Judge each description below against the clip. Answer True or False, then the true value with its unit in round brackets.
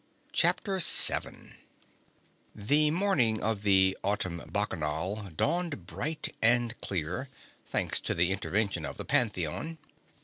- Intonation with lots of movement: True (6.1 semitones)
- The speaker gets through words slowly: True (110 wpm)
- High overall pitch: False (105 Hz)